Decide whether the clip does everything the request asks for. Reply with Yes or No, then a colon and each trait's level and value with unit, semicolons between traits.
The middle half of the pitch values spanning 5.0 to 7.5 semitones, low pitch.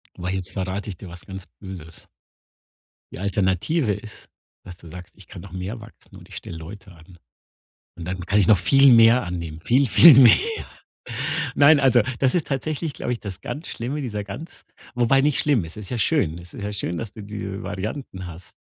Yes: average, 5.3 semitones; low, 100 Hz